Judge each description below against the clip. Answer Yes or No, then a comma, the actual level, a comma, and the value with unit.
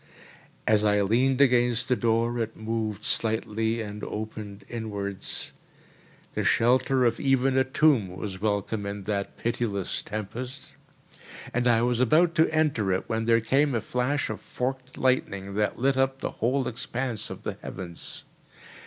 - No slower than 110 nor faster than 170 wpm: Yes, average, 155 wpm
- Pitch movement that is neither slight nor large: Yes, average, 3.5 semitones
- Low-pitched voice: Yes, low, 115 Hz